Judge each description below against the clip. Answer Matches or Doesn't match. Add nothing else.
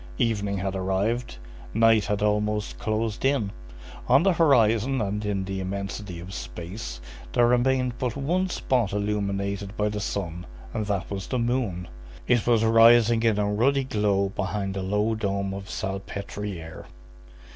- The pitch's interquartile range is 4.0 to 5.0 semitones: Doesn't match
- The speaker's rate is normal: Matches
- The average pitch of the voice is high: Doesn't match